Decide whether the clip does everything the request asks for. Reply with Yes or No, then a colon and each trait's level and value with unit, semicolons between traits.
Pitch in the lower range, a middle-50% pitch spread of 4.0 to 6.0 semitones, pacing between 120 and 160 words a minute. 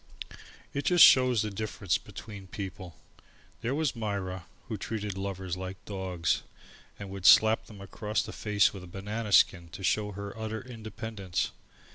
No: low, 100 Hz; narrow, 2.6 semitones; average, 155 wpm